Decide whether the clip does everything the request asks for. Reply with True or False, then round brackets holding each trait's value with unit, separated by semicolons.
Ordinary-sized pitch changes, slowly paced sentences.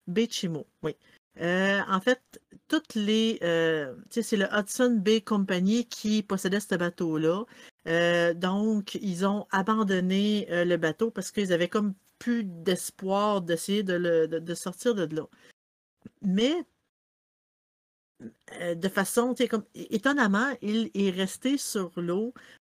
True (4.2 semitones; 130 wpm)